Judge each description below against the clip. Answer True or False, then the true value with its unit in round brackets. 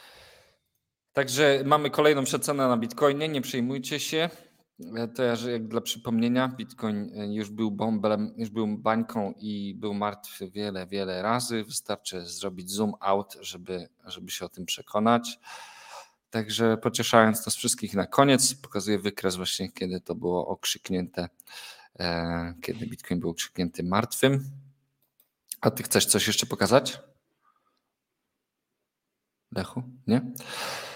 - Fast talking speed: False (125 wpm)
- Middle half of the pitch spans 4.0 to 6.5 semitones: True (4.5 semitones)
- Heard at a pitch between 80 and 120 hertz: True (110 Hz)